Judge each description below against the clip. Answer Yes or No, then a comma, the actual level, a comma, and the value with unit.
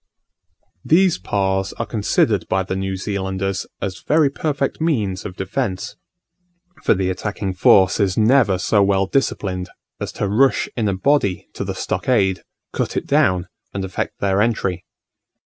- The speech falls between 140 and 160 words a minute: Yes, average, 150 wpm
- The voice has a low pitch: Yes, low, 100 Hz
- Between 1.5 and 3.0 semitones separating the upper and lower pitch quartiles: No, average, 3.9 semitones